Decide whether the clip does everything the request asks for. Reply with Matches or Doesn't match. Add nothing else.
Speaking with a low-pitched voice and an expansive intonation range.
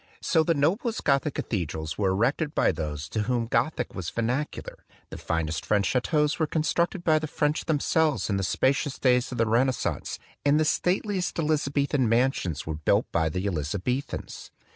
Matches